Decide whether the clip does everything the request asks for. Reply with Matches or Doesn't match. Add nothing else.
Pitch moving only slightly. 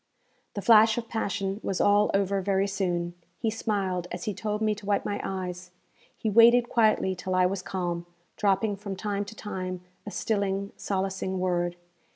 Matches